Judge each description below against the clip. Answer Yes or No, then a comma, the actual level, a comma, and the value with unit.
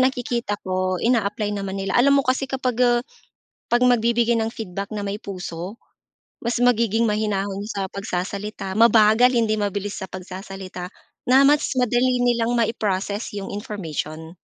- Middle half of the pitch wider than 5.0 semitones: No, average, 3.6 semitones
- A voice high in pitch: Yes, high, 215 Hz